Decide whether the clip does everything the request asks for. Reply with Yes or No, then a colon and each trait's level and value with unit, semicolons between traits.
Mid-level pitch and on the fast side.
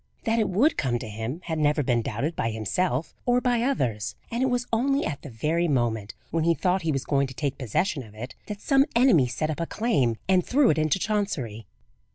Yes: medium, 155 Hz; fast, 225 wpm